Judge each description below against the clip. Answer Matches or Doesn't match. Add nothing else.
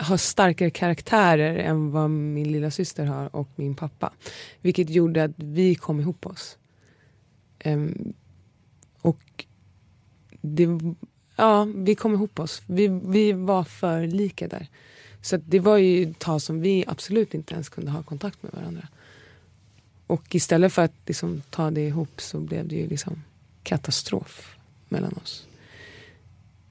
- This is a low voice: Doesn't match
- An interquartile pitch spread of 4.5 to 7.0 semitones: Matches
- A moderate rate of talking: Matches